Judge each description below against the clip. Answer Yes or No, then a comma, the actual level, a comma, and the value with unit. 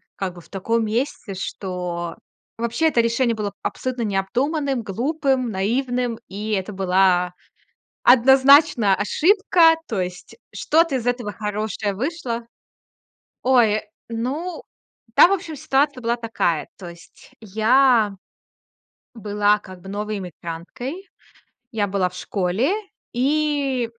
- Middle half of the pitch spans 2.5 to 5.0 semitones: No, wide, 5.4 semitones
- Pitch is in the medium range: No, high, 230 Hz